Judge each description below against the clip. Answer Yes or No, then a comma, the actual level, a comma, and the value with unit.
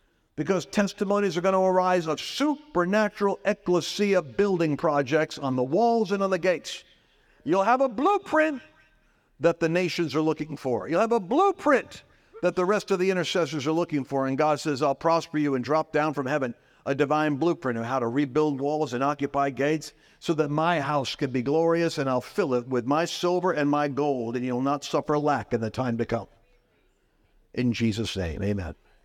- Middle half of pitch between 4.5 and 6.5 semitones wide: Yes, average, 4.8 semitones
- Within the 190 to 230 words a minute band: Yes, average, 195 wpm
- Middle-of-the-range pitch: Yes, medium, 155 Hz